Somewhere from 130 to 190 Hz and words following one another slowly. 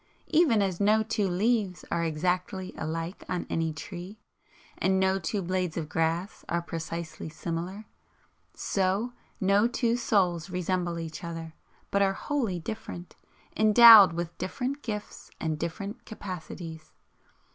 Yes: medium, 185 Hz; slow, 130 wpm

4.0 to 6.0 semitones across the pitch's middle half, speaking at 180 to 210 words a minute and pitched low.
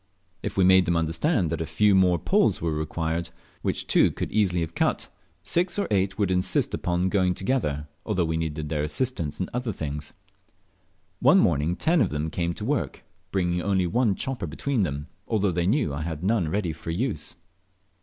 Yes: average, 4.4 semitones; average, 190 wpm; very low, 90 Hz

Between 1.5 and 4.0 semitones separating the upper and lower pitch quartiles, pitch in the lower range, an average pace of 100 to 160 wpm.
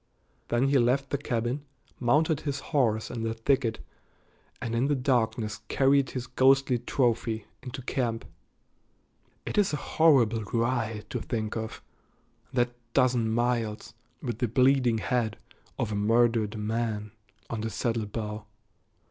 Yes: average, 2.8 semitones; low, 120 Hz; average, 140 wpm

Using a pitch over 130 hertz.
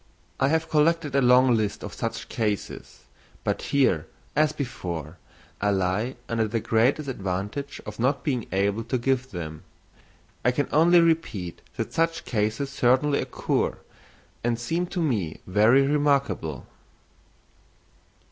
No: low, 125 Hz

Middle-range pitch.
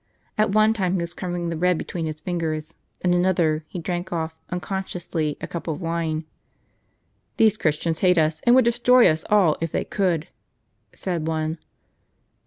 Yes: medium, 175 Hz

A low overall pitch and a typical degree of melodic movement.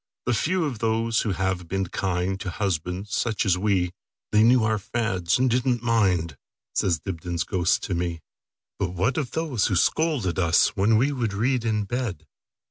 Yes: low, 100 Hz; average, 4.6 semitones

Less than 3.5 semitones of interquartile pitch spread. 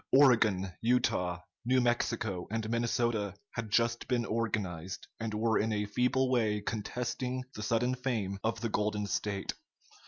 Yes: average, 2.7 semitones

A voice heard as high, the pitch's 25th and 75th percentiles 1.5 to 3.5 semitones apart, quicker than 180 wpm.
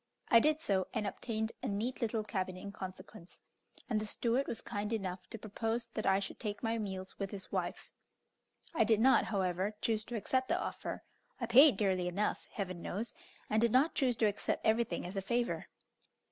Yes: high, 215 Hz; average, 3.2 semitones; average, 195 wpm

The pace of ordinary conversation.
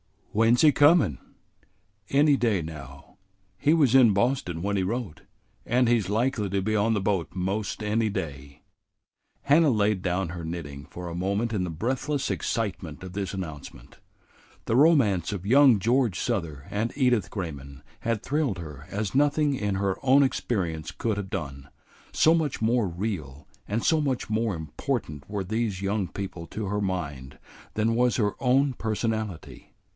Yes: average, 165 wpm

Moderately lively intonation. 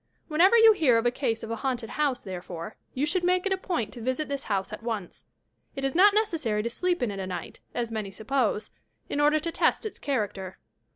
No: wide, 6.6 semitones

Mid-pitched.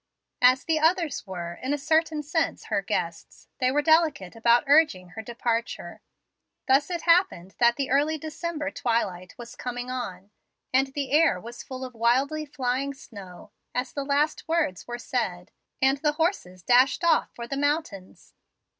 No: very high, 265 Hz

